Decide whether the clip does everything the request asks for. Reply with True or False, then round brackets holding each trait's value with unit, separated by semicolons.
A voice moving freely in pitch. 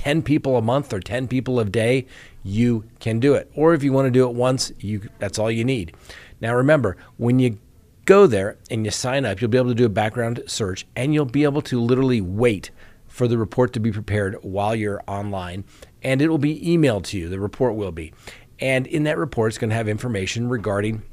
False (3.8 semitones)